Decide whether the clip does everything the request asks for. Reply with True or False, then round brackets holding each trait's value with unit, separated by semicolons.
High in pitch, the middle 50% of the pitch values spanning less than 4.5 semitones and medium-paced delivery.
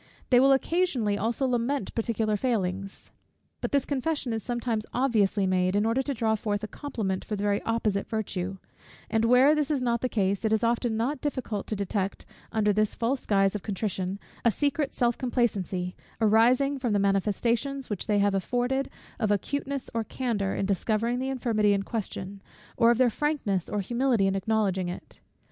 True (225 Hz; 3.9 semitones; 185 wpm)